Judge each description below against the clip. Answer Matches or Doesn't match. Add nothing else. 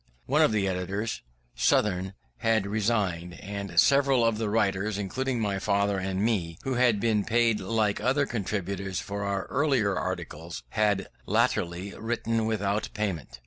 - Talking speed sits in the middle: Matches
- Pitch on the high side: Doesn't match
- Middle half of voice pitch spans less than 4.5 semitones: Matches